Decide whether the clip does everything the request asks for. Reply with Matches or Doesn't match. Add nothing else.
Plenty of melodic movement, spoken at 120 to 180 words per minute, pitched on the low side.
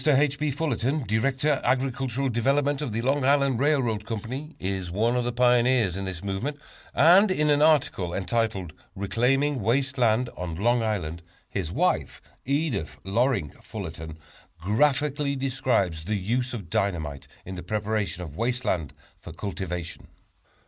Matches